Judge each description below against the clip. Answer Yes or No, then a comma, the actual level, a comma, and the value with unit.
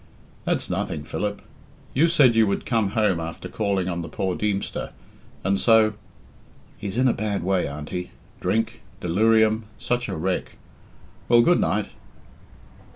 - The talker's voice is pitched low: Yes, low, 105 Hz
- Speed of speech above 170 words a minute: No, average, 150 wpm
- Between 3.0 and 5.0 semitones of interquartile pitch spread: Yes, average, 3.5 semitones